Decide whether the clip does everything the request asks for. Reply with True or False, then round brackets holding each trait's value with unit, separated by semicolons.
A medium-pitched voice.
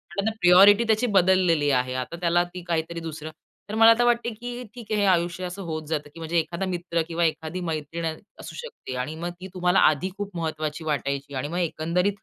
True (170 Hz)